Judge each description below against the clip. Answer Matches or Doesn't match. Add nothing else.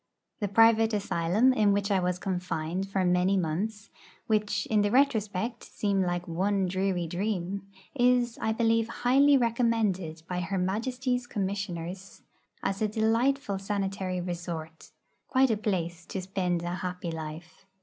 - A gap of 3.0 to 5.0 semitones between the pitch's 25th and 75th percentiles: Matches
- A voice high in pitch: Matches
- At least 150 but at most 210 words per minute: Doesn't match